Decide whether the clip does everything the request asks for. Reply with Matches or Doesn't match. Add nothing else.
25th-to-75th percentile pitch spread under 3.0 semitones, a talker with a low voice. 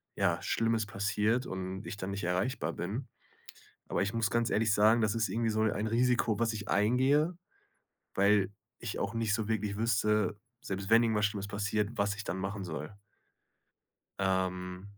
Matches